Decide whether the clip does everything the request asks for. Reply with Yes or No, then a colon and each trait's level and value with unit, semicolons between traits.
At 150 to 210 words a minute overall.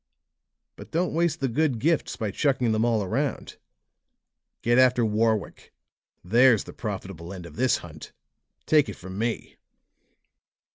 No: average, 140 wpm